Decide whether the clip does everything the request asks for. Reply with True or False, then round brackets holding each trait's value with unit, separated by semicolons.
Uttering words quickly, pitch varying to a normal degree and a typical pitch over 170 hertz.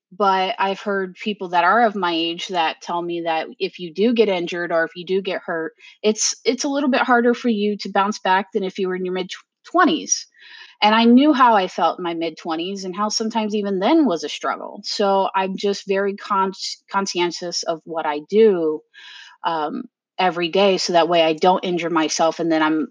True (220 wpm; 3.7 semitones; 190 Hz)